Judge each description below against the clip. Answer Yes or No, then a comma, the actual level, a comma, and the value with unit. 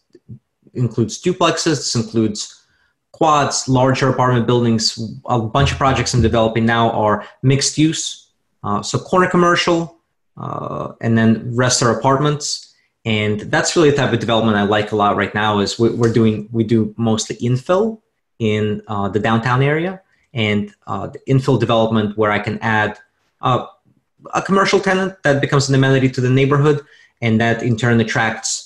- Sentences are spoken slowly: No, average, 160 wpm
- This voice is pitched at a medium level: No, low, 120 Hz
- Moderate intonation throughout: Yes, average, 4.2 semitones